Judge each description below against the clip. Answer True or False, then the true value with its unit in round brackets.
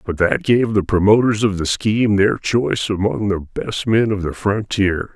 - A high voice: False (105 Hz)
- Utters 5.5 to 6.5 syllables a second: False (4.7 syllables/s)